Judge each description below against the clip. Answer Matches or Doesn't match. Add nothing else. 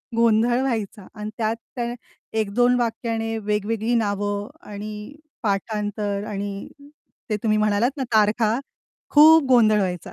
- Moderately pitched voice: Doesn't match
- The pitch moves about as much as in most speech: Doesn't match